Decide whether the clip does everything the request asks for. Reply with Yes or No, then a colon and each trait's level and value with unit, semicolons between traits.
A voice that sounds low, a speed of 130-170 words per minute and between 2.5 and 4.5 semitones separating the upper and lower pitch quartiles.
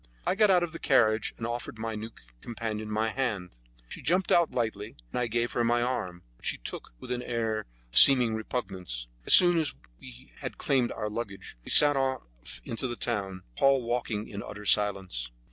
No: low, 115 Hz; average, 195 wpm; average, 3.7 semitones